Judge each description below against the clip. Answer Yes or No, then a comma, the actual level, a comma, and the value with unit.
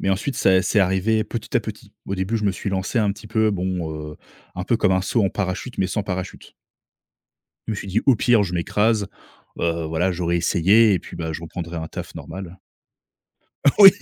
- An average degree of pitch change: Yes, average, 3.3 semitones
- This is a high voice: No, very low, 95 Hz